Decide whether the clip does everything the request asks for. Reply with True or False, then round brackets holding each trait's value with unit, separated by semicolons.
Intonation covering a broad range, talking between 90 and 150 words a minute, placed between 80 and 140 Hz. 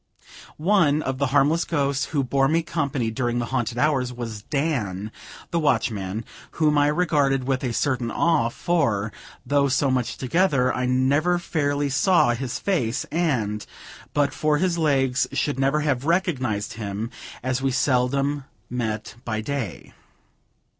False (3.7 semitones; 145 wpm; 135 Hz)